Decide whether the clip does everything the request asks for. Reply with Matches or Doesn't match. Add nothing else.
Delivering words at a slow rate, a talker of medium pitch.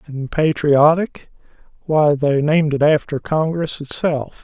Matches